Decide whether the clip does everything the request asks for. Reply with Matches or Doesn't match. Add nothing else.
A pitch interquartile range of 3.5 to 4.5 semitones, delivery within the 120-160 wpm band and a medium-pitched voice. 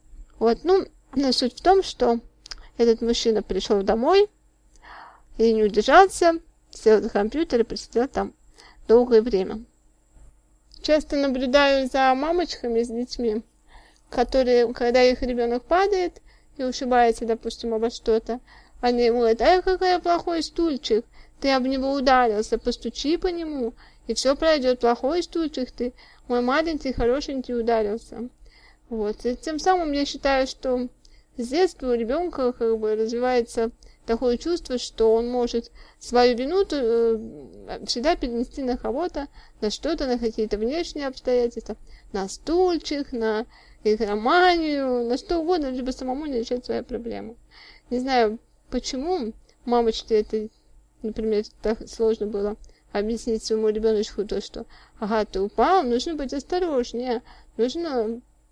Doesn't match